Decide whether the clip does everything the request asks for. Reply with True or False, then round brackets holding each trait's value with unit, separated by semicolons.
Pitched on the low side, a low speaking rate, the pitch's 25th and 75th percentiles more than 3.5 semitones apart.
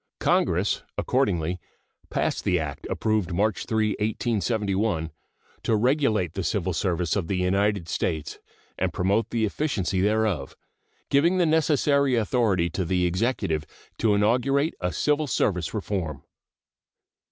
True (105 Hz; 125 wpm; 4.5 semitones)